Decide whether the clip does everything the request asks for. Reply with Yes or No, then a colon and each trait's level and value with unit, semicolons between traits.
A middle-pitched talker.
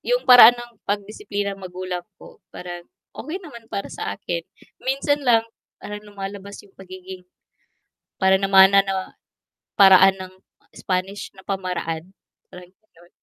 No: high, 195 Hz